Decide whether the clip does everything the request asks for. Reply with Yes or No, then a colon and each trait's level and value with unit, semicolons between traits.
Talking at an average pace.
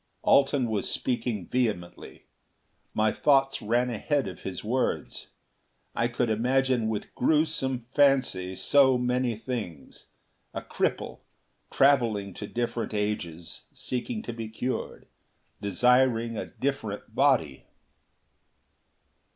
No: slow, 105 wpm